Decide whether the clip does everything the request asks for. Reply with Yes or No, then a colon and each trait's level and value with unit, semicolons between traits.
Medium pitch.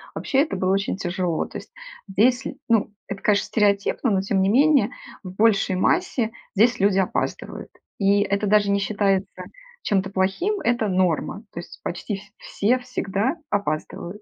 No: high, 200 Hz